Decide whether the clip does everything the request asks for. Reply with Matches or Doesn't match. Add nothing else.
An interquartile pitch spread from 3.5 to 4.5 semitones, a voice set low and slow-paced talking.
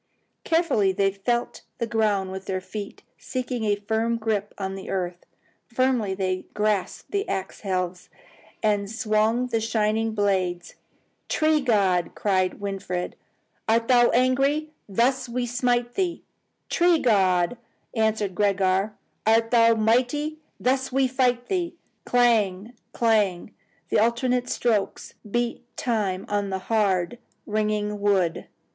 Doesn't match